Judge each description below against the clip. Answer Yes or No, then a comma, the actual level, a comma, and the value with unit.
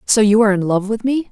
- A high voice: Yes, high, 215 Hz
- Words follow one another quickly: Yes, fast, 320 wpm